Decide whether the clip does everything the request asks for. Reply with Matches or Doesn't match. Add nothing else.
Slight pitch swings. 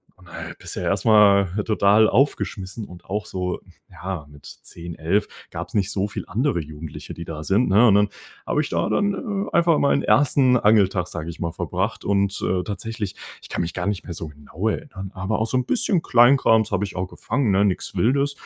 Doesn't match